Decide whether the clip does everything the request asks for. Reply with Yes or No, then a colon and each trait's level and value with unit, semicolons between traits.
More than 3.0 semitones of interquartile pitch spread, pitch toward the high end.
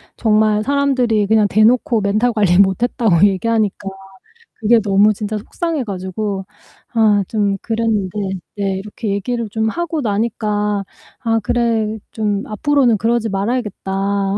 No: narrow, 2.4 semitones; high, 215 Hz